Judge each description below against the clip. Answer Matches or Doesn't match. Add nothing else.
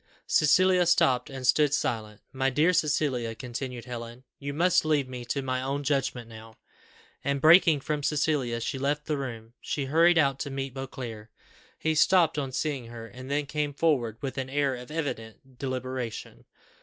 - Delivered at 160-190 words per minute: Matches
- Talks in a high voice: Doesn't match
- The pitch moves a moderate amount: Matches